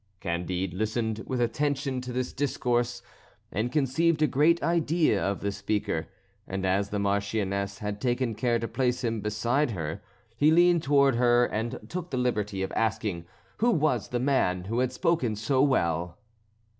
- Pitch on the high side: No, low, 120 Hz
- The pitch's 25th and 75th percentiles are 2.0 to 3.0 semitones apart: No, average, 5.1 semitones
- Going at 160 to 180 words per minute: Yes, average, 165 wpm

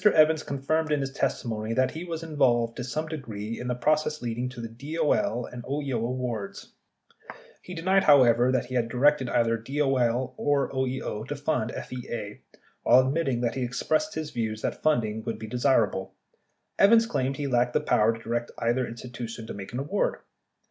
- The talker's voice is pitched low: Yes, low, 125 Hz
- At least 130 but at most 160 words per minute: No, average, 180 wpm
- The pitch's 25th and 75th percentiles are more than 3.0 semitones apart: Yes, average, 4.1 semitones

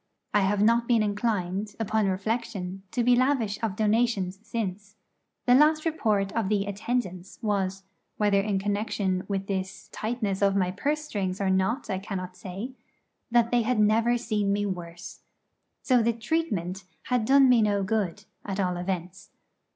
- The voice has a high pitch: Yes, high, 205 Hz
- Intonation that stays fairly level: No, average, 3.3 semitones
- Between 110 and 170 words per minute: Yes, average, 160 wpm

